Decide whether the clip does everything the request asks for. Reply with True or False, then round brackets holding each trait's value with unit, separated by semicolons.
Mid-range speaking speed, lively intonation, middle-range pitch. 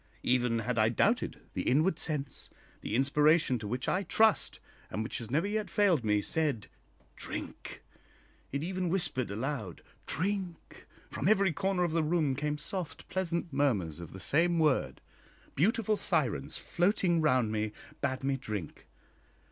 True (150 wpm; 6.3 semitones; 150 Hz)